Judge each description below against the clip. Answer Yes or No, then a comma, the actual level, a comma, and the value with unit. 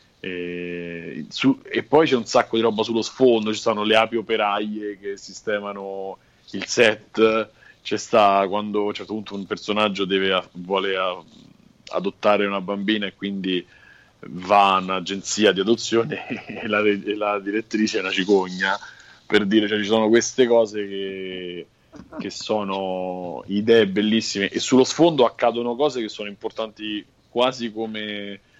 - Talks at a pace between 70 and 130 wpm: No, average, 155 wpm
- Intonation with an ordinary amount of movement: No, narrow, 2.3 semitones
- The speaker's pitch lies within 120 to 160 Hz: No, low, 105 Hz